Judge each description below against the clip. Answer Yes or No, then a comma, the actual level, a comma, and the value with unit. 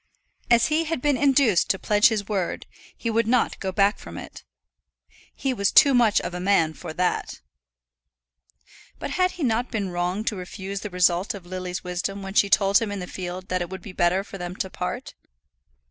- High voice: Yes, high, 200 Hz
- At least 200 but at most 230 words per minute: Yes, fast, 205 wpm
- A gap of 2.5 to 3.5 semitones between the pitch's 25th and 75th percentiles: No, average, 3.9 semitones